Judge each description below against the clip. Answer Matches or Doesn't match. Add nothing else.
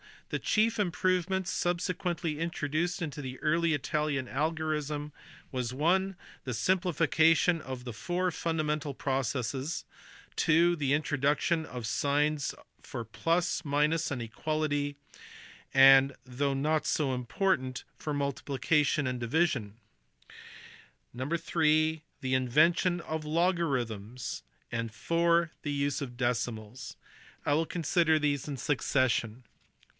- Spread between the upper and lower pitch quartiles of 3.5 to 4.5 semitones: Matches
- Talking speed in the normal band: Doesn't match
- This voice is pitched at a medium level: Matches